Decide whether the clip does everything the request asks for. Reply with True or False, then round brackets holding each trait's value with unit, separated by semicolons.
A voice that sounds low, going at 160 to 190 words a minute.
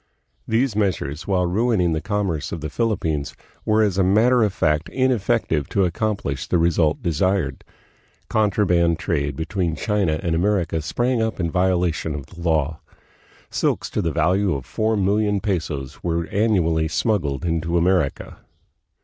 False (90 Hz; 150 wpm)